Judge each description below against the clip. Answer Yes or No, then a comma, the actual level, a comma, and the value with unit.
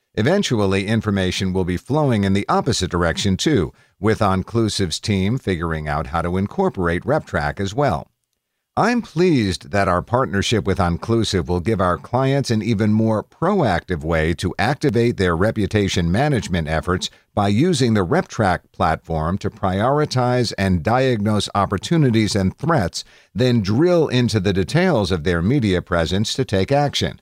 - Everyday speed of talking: Yes, average, 150 wpm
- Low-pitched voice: Yes, low, 100 Hz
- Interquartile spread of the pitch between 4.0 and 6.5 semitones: Yes, average, 5.1 semitones